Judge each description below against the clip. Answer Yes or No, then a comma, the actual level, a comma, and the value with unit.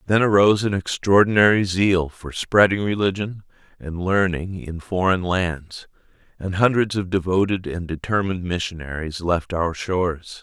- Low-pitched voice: Yes, very low, 95 Hz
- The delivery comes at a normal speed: No, slow, 130 wpm